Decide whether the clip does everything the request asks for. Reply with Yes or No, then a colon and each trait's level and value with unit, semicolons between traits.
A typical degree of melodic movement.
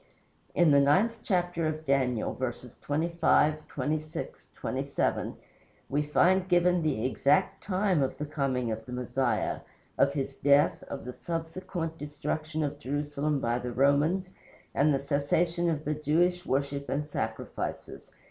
Yes: average, 3.3 semitones